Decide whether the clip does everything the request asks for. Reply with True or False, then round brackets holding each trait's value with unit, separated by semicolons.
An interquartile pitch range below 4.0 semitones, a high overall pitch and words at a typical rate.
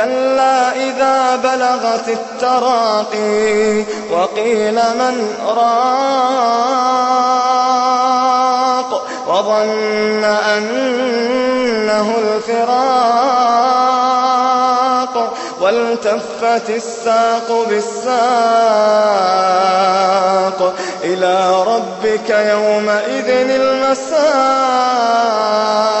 False (2.9 semitones; 235 Hz; 40 wpm)